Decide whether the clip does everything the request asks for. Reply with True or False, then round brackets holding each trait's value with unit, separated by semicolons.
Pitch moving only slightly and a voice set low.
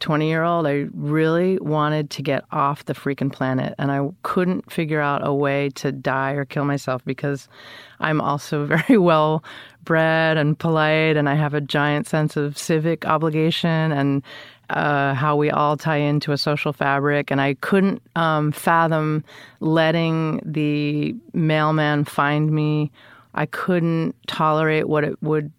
False (1.9 semitones; 150 Hz)